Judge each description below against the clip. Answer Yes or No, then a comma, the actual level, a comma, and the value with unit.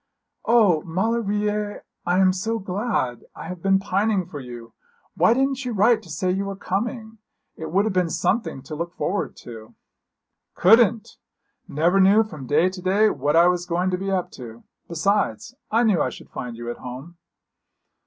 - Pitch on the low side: No, medium, 185 Hz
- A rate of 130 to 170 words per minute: No, average, 180 wpm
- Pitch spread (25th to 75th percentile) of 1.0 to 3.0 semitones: No, average, 4.6 semitones